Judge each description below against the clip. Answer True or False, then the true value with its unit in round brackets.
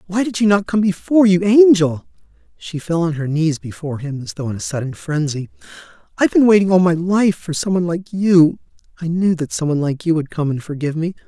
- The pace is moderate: False (235 wpm)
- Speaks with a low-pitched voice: False (170 Hz)